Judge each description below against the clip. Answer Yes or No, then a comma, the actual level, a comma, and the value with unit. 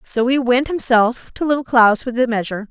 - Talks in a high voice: Yes, high, 245 Hz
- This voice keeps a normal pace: No, fast, 220 wpm